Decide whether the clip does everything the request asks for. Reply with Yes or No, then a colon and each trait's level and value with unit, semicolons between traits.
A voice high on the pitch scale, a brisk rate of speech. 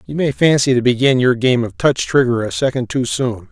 No: low, 125 Hz; fast, 240 wpm